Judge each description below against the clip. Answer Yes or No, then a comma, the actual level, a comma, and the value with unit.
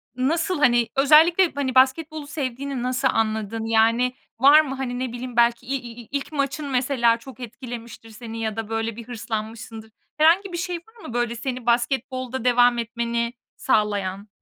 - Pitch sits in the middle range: No, high, 245 Hz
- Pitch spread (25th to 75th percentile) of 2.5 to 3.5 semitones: Yes, average, 3.2 semitones